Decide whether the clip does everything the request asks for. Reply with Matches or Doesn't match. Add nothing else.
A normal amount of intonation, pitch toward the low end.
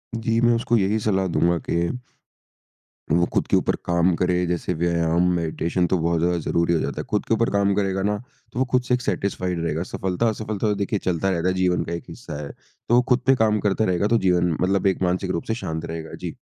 Matches